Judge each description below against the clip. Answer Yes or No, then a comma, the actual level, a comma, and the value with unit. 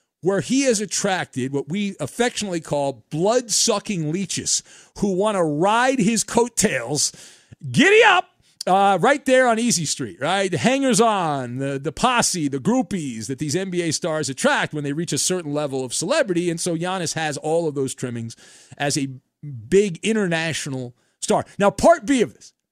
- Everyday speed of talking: Yes, average, 170 wpm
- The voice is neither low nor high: Yes, medium, 175 Hz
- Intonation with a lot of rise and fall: Yes, wide, 6.3 semitones